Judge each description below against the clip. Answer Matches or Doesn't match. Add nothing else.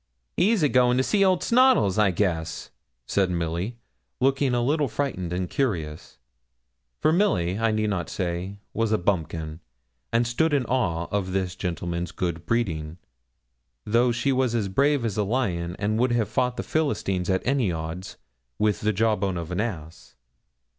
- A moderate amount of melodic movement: Doesn't match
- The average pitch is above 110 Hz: Doesn't match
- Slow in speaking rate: Doesn't match